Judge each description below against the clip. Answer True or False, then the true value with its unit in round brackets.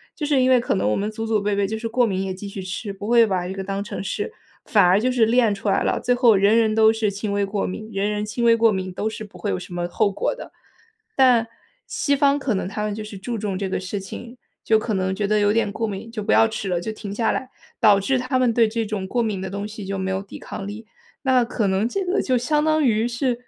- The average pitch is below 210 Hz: False (215 Hz)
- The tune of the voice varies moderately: True (3.0 semitones)